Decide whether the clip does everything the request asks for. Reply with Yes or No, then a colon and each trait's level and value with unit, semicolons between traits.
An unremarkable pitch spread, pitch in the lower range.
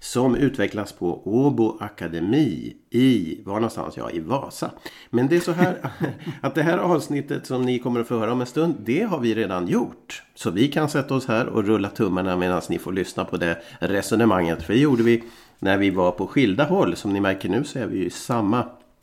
No: wide, 5.7 semitones; low, 115 Hz